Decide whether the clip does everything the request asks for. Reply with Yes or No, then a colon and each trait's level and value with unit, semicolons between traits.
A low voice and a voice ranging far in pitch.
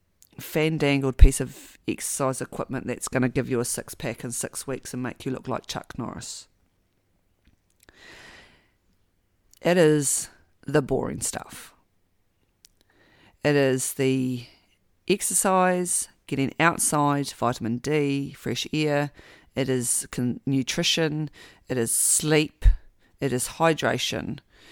Yes: low, 130 Hz; wide, 6.7 semitones